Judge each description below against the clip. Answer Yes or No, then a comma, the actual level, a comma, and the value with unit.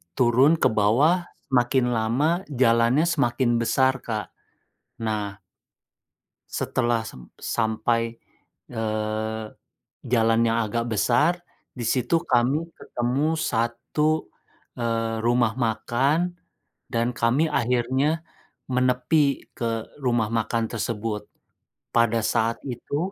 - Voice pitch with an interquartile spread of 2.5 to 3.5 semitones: Yes, average, 2.8 semitones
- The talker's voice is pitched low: Yes, low, 120 Hz